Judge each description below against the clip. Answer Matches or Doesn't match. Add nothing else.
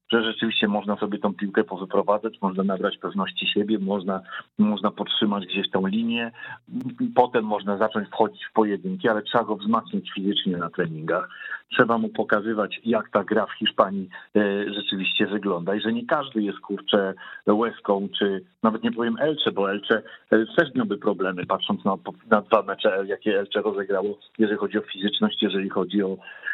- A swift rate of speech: Matches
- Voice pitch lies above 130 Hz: Doesn't match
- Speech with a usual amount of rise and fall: Doesn't match